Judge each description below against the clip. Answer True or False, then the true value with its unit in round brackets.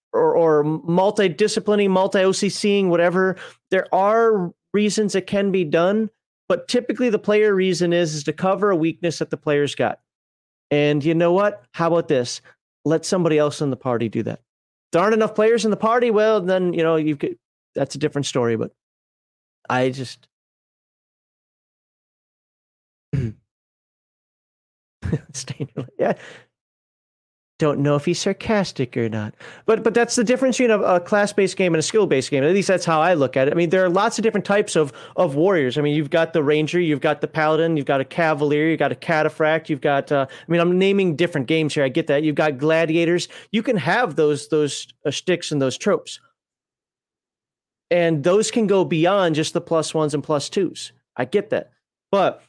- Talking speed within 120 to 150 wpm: False (190 wpm)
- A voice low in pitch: False (170 Hz)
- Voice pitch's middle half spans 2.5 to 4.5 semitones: False (4.9 semitones)